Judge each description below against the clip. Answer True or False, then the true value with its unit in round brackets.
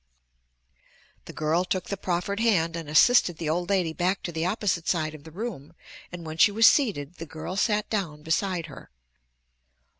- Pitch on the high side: False (175 Hz)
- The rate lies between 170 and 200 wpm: True (180 wpm)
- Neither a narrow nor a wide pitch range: True (3.8 semitones)